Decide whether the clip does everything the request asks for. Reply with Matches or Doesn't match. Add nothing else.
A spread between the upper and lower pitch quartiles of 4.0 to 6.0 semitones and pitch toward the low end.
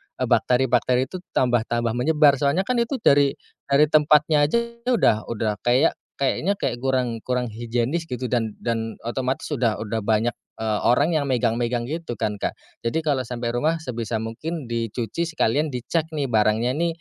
Matches